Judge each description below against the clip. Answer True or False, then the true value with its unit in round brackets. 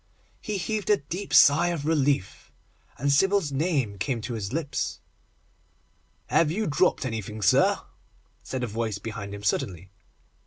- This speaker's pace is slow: False (145 wpm)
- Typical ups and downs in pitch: False (7.6 semitones)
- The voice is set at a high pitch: False (140 Hz)